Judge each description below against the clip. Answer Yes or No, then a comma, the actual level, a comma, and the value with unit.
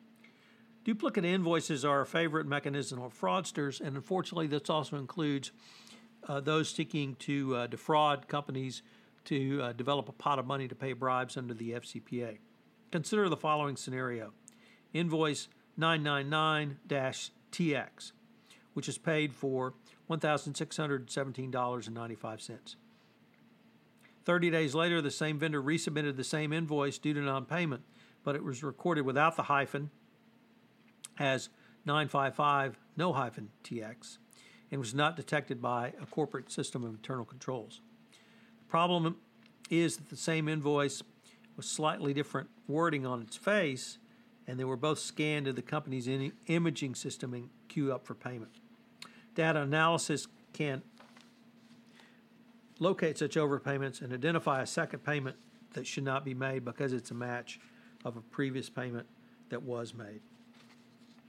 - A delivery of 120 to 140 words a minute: Yes, slow, 135 wpm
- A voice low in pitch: No, medium, 150 Hz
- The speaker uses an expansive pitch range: No, average, 4.6 semitones